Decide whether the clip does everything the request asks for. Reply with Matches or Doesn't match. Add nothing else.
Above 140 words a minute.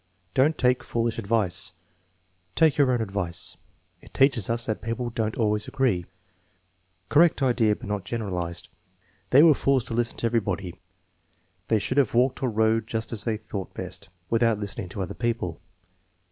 Matches